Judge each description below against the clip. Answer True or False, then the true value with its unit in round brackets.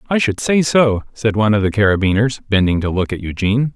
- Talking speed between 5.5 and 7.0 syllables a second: True (6.0 syllables/s)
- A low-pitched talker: True (110 Hz)